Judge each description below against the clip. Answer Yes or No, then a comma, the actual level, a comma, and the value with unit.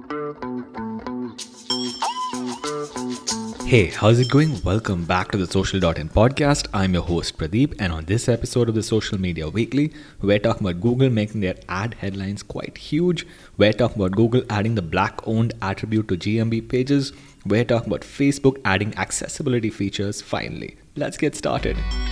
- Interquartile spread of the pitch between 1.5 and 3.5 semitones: No, average, 4.2 semitones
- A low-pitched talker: Yes, low, 110 Hz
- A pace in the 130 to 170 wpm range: Yes, average, 150 wpm